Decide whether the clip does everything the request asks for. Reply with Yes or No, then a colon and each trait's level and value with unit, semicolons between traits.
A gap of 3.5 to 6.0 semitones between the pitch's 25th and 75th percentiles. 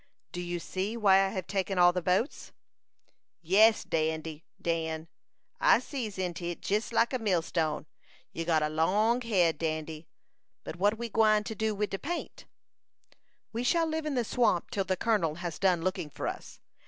Yes: average, 4.8 semitones